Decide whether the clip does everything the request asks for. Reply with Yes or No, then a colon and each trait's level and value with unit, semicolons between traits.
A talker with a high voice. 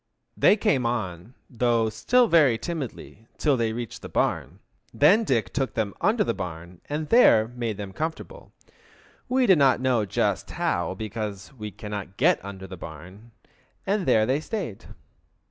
No: low, 115 Hz